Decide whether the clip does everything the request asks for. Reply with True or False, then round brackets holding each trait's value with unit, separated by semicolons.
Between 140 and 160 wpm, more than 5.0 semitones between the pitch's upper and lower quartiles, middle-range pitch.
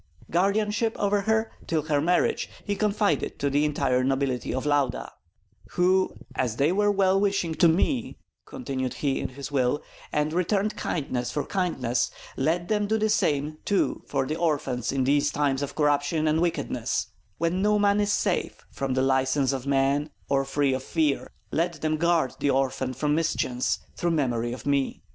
False (175 wpm; 5.5 semitones; 150 Hz)